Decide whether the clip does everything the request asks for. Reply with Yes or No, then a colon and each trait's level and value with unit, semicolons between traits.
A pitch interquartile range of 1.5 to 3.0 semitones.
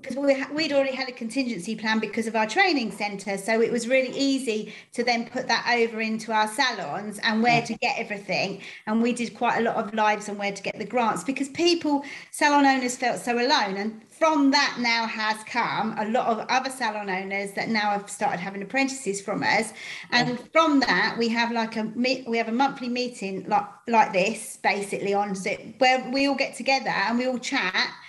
No: average, 3.6 semitones